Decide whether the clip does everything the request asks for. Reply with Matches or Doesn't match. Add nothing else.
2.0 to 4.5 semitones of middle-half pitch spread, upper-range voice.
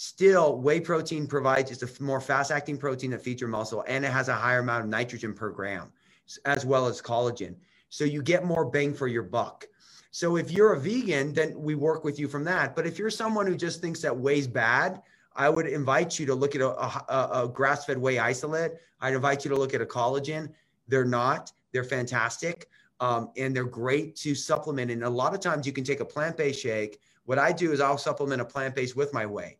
Doesn't match